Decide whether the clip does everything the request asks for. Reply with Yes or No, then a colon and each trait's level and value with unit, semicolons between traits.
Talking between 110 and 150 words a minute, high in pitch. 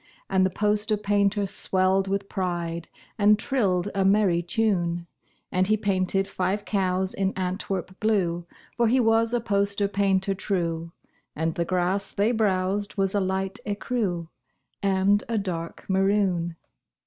Yes: average, 140 wpm; high, 195 Hz